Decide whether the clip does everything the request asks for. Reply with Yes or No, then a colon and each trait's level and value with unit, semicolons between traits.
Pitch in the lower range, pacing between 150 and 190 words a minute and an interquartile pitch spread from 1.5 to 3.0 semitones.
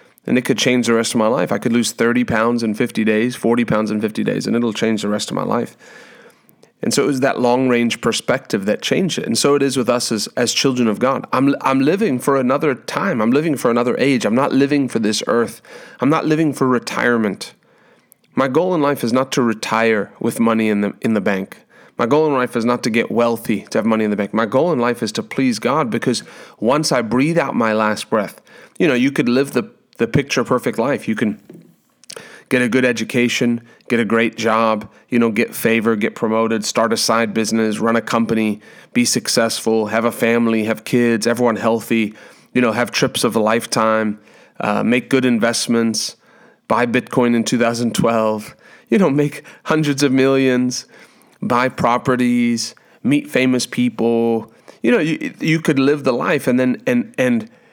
No: low, 120 Hz; fast, 205 wpm; narrow, 2.6 semitones